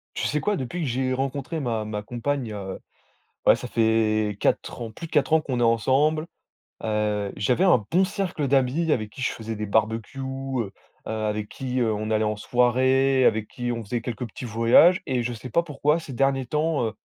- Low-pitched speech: Yes, low, 125 Hz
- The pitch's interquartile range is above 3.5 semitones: Yes, average, 3.9 semitones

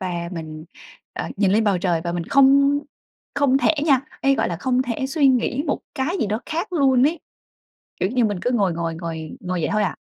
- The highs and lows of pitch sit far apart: Yes, wide, 7.6 semitones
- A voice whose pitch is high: Yes, high, 230 Hz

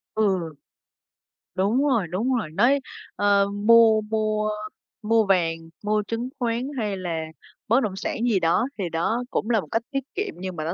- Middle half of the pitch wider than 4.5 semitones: No, average, 3.7 semitones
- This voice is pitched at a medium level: No, high, 215 Hz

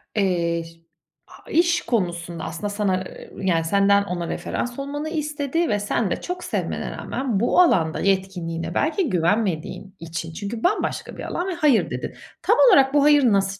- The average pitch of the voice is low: No, high, 200 Hz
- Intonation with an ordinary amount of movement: No, wide, 8.5 semitones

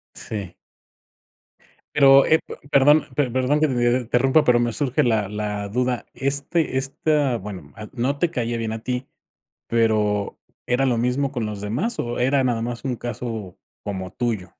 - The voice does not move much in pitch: No, average, 3.7 semitones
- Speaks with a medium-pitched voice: No, low, 120 Hz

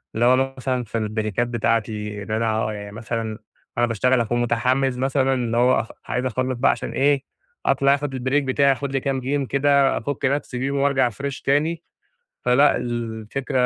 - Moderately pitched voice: No, low, 130 Hz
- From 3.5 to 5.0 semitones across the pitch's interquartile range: No, average, 3.0 semitones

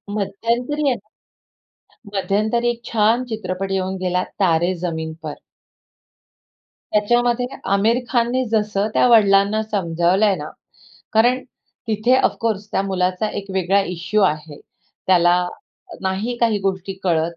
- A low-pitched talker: No, high, 200 Hz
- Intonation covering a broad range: No, average, 3.7 semitones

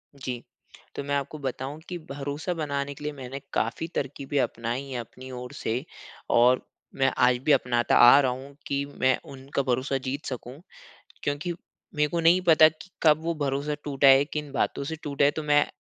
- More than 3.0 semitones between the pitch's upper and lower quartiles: No, narrow, 2.4 semitones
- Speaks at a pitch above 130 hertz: Yes, medium, 140 Hz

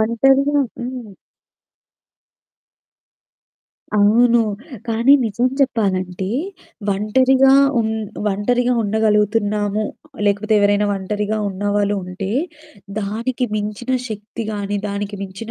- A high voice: Yes, high, 210 Hz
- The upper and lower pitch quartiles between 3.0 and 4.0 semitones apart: No, narrow, 2.6 semitones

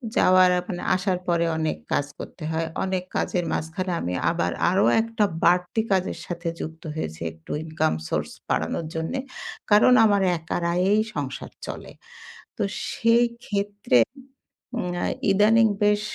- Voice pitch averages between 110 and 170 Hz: No, medium, 180 Hz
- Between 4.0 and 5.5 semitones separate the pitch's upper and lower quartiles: Yes, average, 4.3 semitones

